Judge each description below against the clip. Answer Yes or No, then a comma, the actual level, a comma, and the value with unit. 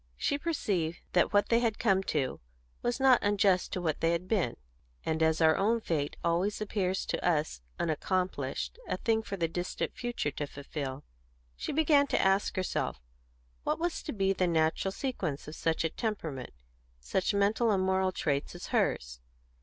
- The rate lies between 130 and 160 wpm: No, average, 175 wpm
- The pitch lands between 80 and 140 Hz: No, medium, 185 Hz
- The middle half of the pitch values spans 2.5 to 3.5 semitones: No, average, 4.9 semitones